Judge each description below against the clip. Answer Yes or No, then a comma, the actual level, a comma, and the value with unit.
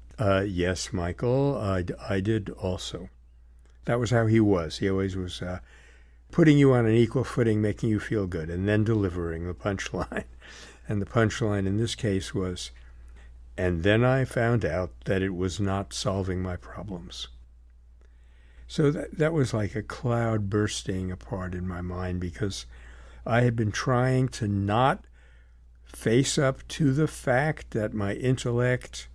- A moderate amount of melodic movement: No, wide, 8.9 semitones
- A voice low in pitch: Yes, very low, 95 Hz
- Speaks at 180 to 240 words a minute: No, average, 160 wpm